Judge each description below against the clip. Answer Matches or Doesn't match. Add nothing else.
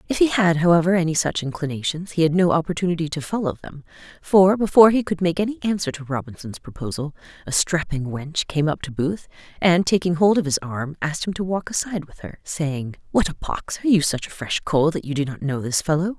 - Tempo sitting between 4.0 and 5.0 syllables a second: Doesn't match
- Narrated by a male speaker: Doesn't match